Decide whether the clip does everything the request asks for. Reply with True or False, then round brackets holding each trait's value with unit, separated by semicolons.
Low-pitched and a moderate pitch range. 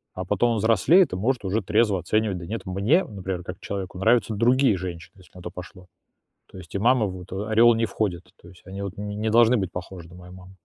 True (100 Hz; 3.4 semitones)